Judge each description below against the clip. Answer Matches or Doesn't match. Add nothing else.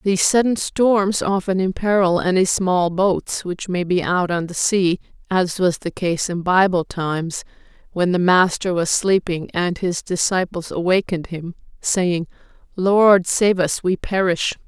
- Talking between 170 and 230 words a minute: Doesn't match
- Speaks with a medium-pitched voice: Matches